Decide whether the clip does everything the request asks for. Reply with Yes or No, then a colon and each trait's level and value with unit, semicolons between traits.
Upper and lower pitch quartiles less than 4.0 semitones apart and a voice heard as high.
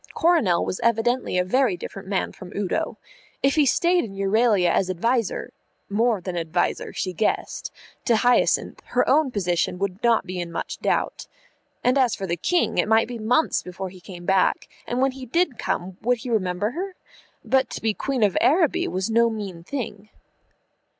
No: average, 5.2 semitones; high, 215 Hz